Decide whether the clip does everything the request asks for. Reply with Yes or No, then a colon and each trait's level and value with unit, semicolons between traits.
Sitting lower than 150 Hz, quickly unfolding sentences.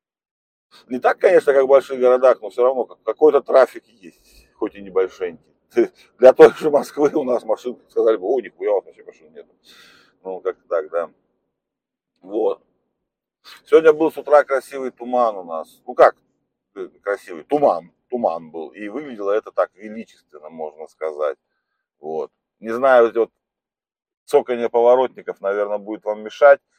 No: medium, 140 Hz; average, 150 wpm